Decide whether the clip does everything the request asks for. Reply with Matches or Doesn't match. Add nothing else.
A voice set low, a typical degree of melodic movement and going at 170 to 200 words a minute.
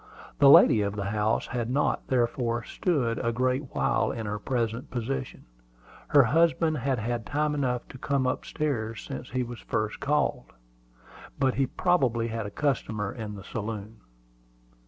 Doesn't match